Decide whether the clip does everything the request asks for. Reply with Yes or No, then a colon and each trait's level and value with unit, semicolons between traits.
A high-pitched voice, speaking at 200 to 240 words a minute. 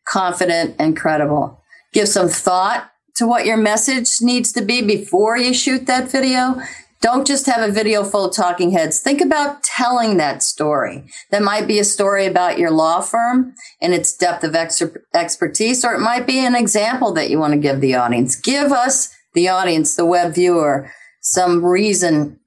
No: high, 205 Hz; average, 185 wpm